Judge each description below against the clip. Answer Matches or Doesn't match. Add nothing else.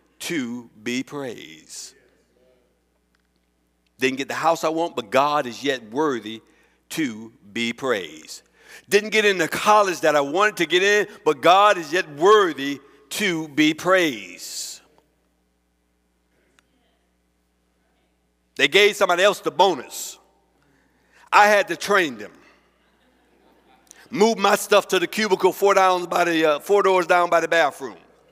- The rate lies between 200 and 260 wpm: Doesn't match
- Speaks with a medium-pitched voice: Matches